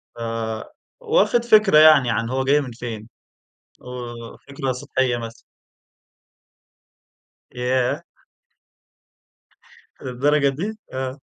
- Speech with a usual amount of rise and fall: Yes, average, 3.6 semitones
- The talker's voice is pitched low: Yes, low, 130 Hz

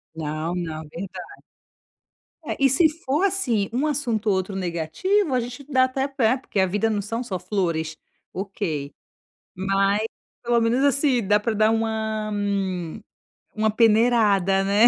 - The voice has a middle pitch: No, high, 215 Hz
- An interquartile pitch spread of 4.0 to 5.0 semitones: Yes, average, 4.5 semitones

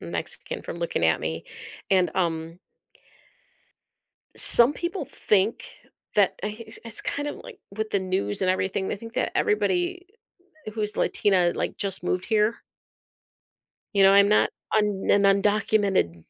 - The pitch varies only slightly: No, average, 3.1 semitones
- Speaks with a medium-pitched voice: No, high, 200 Hz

